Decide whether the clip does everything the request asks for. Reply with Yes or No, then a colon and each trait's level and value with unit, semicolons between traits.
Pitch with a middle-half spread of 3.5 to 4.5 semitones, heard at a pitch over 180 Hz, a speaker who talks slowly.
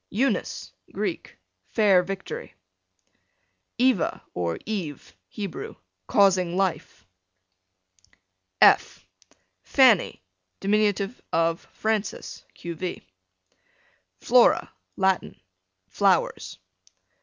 Yes: average, 3.8 semitones; high, 190 Hz; slow, 65 wpm